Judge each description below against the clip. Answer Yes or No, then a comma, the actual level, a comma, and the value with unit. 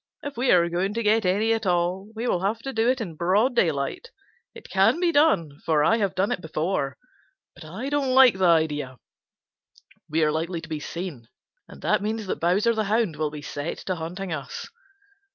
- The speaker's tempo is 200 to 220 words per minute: Yes, fast, 205 wpm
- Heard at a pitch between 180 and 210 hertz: Yes, medium, 185 Hz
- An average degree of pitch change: No, wide, 5.8 semitones